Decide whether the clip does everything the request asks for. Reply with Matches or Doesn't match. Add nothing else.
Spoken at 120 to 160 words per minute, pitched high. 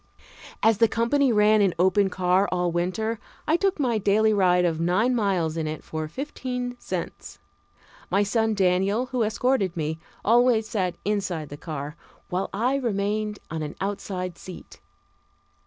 Matches